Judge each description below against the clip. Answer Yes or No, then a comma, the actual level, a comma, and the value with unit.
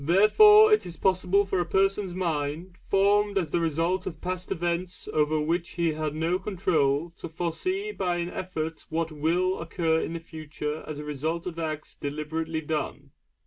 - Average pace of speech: Yes, average, 175 wpm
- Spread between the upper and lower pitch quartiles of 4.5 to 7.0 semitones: No, average, 2.9 semitones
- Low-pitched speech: No, medium, 170 Hz